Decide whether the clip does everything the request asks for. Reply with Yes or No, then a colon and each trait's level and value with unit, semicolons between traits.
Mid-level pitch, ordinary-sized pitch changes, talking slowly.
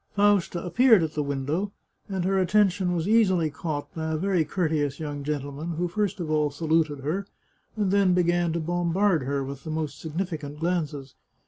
No: medium, 165 Hz; average, 3.8 semitones; average, 175 wpm